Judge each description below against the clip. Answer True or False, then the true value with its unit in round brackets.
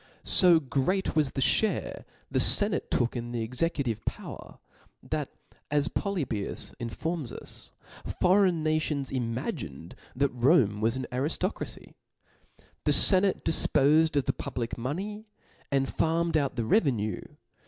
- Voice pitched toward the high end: False (140 Hz)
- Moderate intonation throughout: False (5.7 semitones)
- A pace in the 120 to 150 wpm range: True (140 wpm)